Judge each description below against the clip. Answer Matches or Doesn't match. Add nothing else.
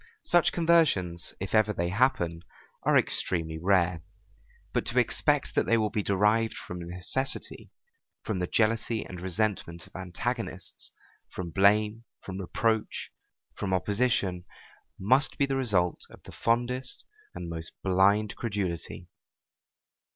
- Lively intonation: Doesn't match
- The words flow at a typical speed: Doesn't match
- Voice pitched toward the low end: Matches